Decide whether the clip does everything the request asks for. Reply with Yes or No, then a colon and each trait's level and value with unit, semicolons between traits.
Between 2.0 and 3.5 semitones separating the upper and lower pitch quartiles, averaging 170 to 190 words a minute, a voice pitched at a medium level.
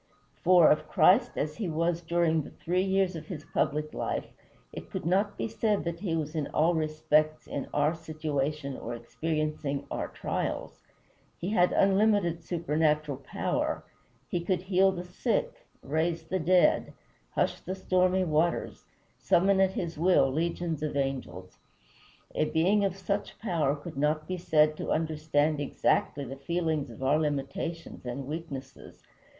No: average, 3.1 semitones; average, 155 wpm; medium, 160 Hz